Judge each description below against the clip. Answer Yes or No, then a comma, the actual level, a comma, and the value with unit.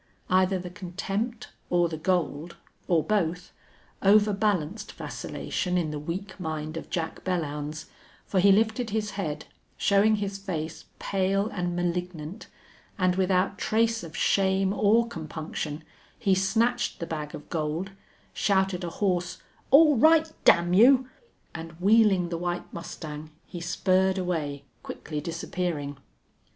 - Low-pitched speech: No, medium, 180 Hz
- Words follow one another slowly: Yes, slow, 130 wpm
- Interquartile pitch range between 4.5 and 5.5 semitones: No, average, 3.4 semitones